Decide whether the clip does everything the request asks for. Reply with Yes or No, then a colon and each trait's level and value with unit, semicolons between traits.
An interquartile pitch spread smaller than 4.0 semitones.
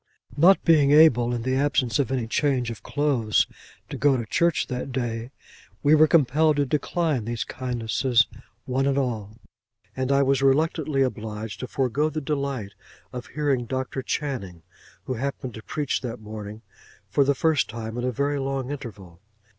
Yes: average, 3.5 semitones